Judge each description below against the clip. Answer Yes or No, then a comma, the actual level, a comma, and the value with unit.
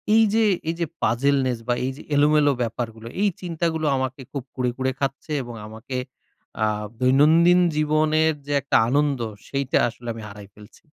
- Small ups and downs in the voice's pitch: No, average, 4.1 semitones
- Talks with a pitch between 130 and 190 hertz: Yes, medium, 140 Hz